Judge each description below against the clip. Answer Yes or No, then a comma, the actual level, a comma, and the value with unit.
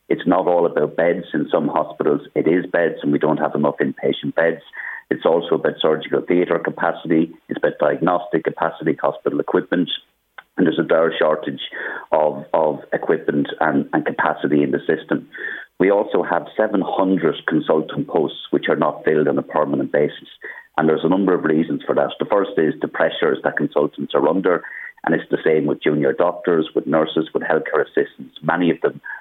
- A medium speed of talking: Yes, average, 185 wpm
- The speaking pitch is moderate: No, very low, 90 Hz